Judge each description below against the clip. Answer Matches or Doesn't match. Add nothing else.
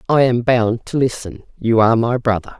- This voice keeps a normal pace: Doesn't match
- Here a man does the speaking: Doesn't match